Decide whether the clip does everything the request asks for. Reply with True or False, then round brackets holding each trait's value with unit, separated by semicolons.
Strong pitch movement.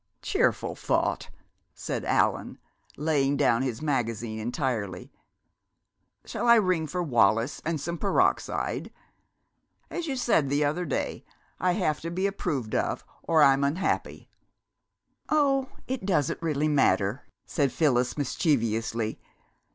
True (6.2 semitones)